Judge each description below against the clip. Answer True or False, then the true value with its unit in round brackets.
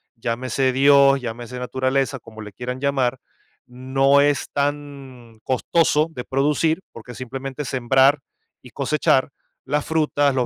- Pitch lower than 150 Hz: True (135 Hz)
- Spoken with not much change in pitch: True (2.2 semitones)